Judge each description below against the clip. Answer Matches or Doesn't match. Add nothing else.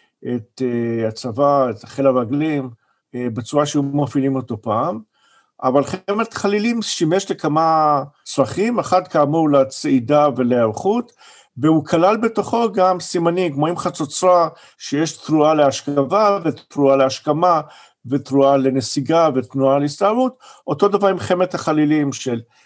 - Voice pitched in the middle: Matches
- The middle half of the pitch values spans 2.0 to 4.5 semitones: Doesn't match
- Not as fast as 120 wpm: Matches